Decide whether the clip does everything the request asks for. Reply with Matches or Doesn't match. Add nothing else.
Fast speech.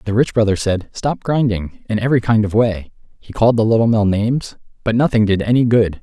Matches